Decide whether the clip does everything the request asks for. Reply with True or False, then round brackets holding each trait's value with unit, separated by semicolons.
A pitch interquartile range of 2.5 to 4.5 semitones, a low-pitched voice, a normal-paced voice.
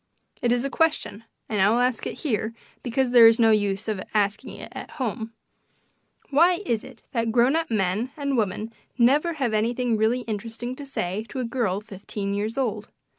False (3.1 semitones; 230 Hz; 190 wpm)